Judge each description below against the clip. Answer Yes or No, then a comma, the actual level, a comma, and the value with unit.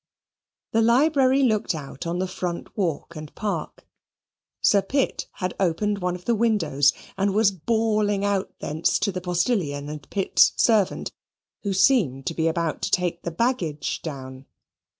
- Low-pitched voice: No, medium, 185 Hz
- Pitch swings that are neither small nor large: Yes, average, 4.9 semitones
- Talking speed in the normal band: Yes, average, 155 wpm